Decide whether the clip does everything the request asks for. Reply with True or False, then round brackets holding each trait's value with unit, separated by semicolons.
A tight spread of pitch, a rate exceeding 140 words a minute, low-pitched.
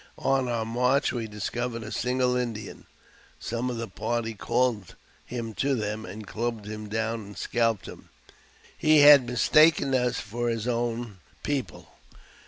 True (2.2 semitones; 150 wpm; 115 Hz)